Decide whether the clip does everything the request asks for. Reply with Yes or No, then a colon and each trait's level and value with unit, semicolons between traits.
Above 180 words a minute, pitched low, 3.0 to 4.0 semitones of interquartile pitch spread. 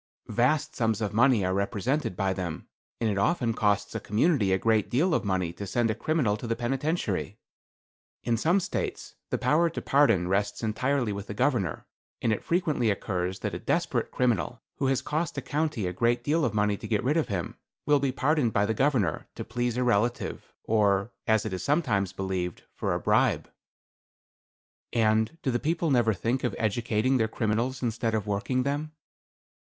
No: average, 190 wpm; low, 115 Hz; average, 4.8 semitones